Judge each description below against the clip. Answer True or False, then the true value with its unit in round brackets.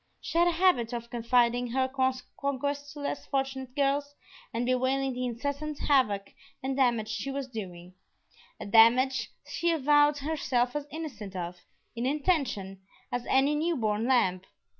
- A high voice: True (260 Hz)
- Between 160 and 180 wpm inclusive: False (150 wpm)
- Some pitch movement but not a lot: True (3.4 semitones)